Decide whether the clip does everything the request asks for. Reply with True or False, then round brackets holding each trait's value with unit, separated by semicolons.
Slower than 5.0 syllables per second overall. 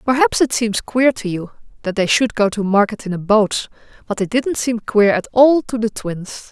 True (4.8 syllables/s)